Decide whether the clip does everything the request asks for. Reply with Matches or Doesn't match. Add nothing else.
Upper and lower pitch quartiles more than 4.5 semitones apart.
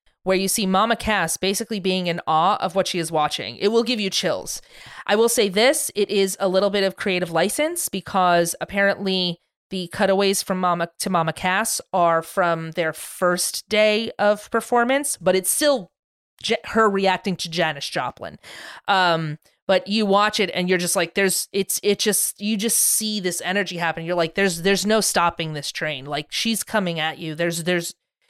Doesn't match